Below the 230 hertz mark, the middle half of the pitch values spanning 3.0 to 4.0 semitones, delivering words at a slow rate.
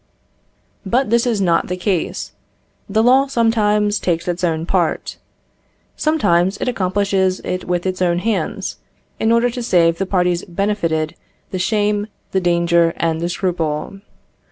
No: medium, 185 Hz; average, 3.5 semitones; average, 145 wpm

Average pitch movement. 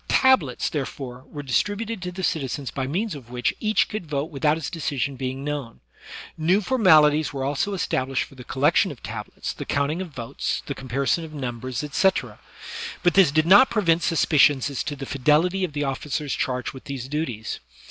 Yes: average, 4.4 semitones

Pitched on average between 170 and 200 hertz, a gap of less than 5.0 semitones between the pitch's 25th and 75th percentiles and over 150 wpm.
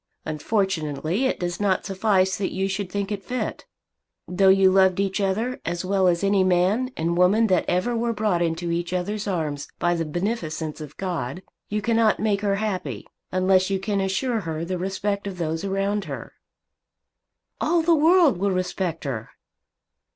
Yes: high, 190 Hz; average, 2.8 semitones; average, 175 wpm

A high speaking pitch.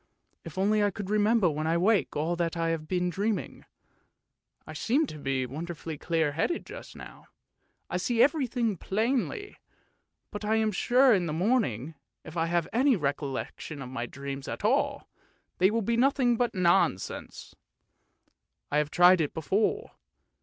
No: medium, 180 Hz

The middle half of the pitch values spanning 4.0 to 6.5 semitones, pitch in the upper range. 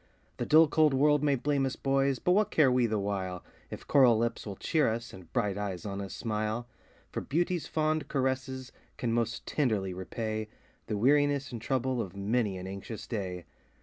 No: average, 5.2 semitones; low, 120 Hz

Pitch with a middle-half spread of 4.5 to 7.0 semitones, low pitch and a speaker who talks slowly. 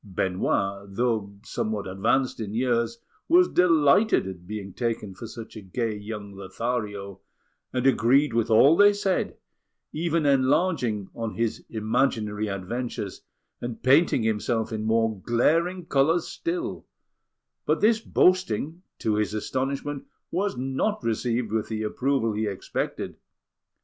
Yes: average, 4.9 semitones; low, 115 Hz; slow, 130 wpm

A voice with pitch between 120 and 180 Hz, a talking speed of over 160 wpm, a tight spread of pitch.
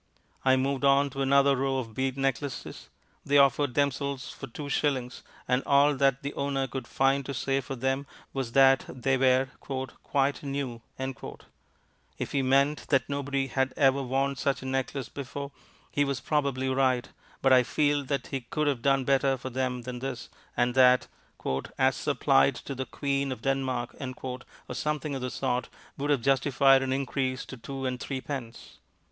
Yes: low, 135 Hz; average, 175 wpm; narrow, 1.3 semitones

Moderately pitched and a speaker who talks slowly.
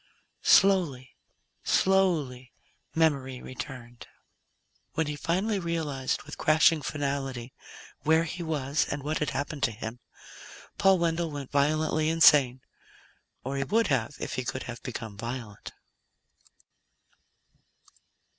Yes: medium, 145 Hz; slow, 115 wpm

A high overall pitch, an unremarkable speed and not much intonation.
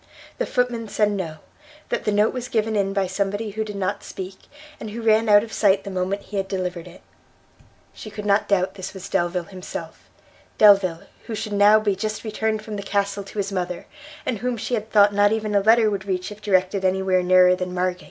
No: high, 200 Hz; fast, 220 wpm; narrow, 2.3 semitones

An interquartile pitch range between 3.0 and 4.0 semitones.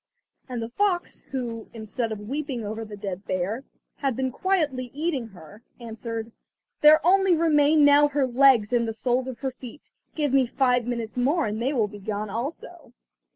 No: average, 4.5 semitones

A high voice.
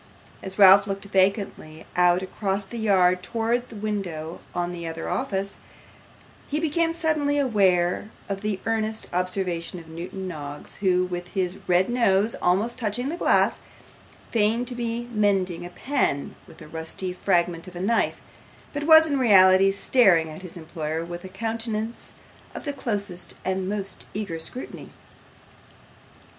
Yes: high, 195 Hz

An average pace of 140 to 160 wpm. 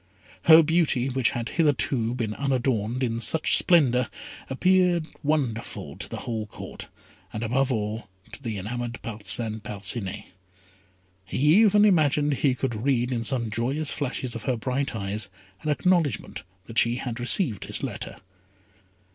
Yes: average, 145 wpm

